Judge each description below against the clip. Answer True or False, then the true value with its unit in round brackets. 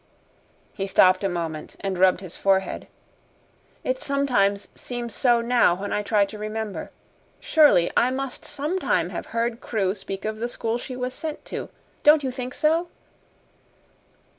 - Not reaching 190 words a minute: True (155 wpm)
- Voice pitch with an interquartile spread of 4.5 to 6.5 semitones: True (4.8 semitones)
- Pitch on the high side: True (230 Hz)